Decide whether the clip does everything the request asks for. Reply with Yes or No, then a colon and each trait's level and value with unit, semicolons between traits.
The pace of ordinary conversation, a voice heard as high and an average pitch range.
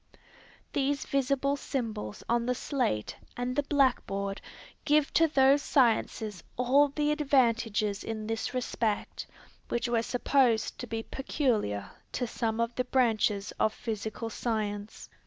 No: slow, 130 wpm; high, 240 Hz; average, 3.9 semitones